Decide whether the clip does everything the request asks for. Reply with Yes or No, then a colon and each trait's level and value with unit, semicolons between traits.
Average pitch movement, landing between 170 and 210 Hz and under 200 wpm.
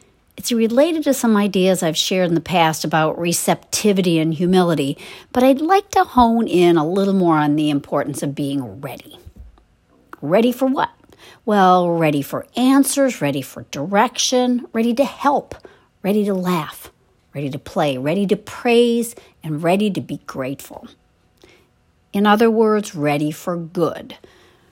No: wide, 7.1 semitones; medium, 185 Hz; average, 150 wpm